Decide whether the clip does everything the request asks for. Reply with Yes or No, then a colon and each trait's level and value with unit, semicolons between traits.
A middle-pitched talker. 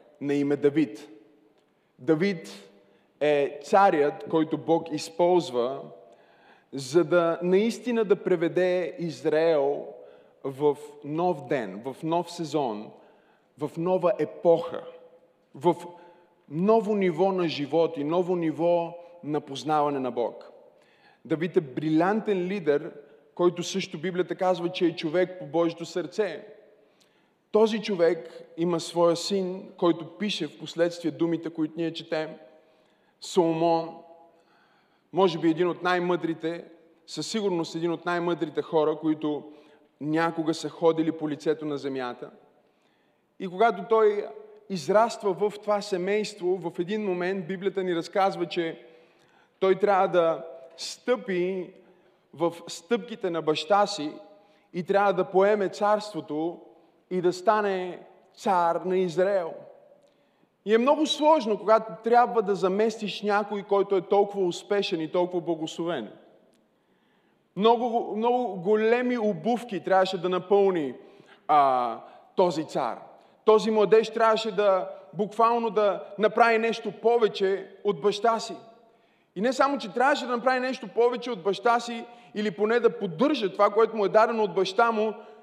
Yes: medium, 180 Hz